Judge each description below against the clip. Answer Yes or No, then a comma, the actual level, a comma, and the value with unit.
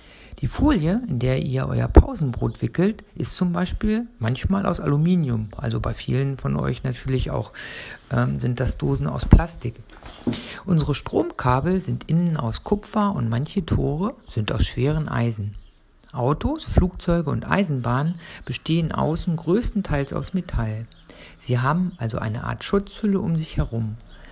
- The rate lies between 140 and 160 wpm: Yes, average, 145 wpm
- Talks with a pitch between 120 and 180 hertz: Yes, medium, 140 Hz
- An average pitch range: No, wide, 7.6 semitones